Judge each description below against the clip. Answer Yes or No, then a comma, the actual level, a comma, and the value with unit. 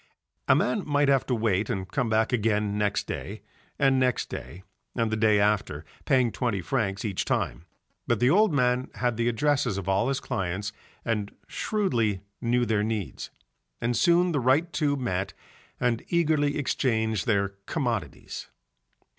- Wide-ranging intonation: No, average, 4.7 semitones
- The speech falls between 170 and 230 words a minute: No, average, 160 wpm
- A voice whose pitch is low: Yes, low, 115 Hz